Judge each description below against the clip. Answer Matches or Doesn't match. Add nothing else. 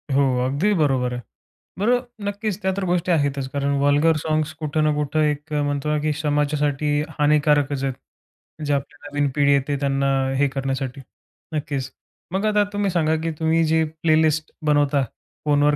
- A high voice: Doesn't match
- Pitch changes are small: Matches